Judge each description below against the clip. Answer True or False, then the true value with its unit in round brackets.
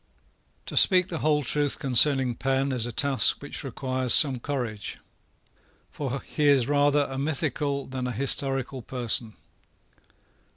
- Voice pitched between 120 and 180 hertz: True (135 Hz)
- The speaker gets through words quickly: False (135 wpm)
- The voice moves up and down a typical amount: False (2.3 semitones)